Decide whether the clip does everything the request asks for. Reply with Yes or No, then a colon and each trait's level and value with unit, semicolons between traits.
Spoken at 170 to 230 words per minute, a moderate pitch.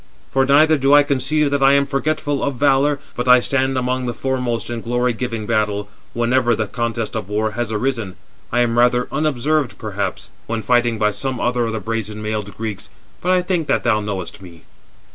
No: average, 200 wpm; low, 120 Hz